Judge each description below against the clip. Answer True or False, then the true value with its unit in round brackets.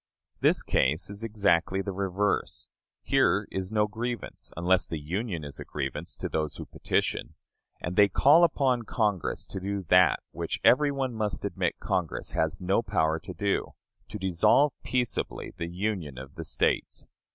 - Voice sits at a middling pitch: False (95 Hz)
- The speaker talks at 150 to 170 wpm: True (165 wpm)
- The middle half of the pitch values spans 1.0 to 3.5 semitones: False (4.3 semitones)